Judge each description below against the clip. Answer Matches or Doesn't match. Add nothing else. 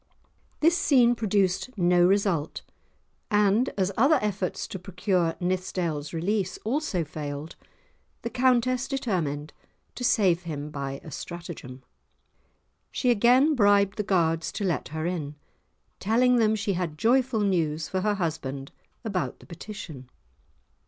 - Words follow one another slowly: Matches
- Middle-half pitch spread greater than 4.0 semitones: Matches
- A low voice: Doesn't match